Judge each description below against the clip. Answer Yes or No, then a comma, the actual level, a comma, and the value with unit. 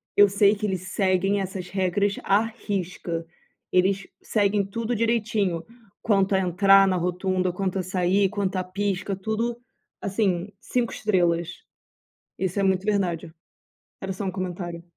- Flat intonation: Yes, narrow, 1.9 semitones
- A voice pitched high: Yes, high, 195 Hz